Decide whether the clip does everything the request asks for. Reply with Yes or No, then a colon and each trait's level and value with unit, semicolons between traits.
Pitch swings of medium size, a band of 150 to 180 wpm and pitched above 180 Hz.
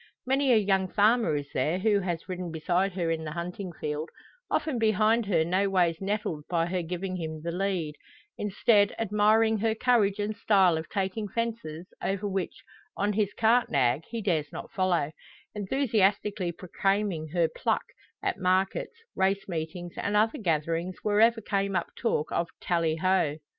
Yes: average, 3.8 semitones; average, 165 wpm; high, 190 Hz